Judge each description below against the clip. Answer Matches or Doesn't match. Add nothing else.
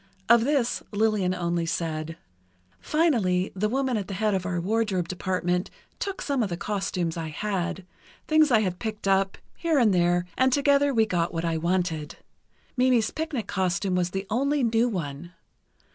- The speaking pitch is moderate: Doesn't match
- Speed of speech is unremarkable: Matches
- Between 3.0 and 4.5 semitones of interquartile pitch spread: Doesn't match